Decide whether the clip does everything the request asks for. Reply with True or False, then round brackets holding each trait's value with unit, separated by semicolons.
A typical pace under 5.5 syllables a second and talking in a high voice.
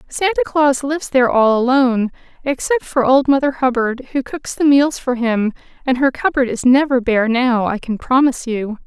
True (5.0 syllables/s; 260 Hz)